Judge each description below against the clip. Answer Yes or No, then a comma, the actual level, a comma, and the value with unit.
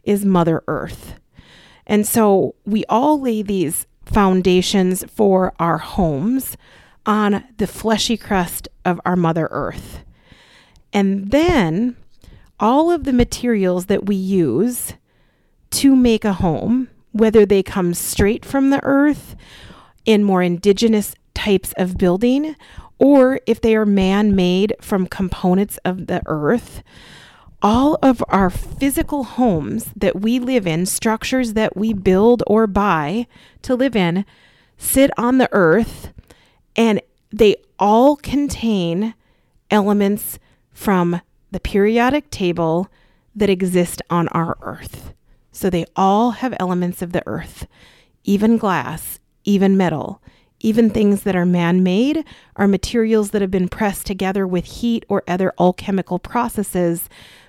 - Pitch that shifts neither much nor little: Yes, average, 4.2 semitones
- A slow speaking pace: Yes, slow, 130 wpm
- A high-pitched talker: Yes, high, 200 Hz